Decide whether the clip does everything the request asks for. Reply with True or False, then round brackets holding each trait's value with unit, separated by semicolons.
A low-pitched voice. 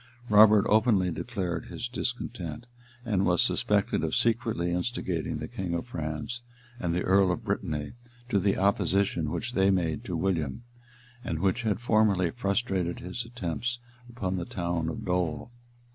True (95 Hz)